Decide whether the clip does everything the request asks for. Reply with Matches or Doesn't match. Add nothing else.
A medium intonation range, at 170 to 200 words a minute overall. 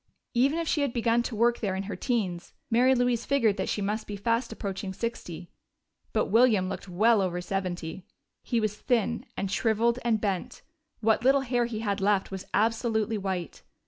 Matches